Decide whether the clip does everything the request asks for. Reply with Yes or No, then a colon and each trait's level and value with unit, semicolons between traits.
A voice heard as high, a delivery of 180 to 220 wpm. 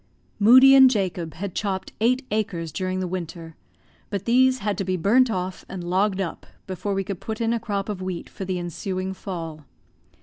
Yes: high, 195 Hz; average, 195 wpm